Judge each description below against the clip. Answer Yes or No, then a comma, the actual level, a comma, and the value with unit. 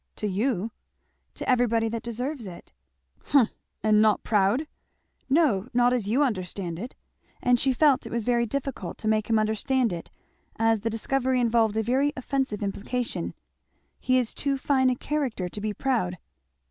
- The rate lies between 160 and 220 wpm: Yes, average, 165 wpm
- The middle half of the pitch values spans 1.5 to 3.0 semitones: No, average, 3.5 semitones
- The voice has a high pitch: Yes, high, 235 Hz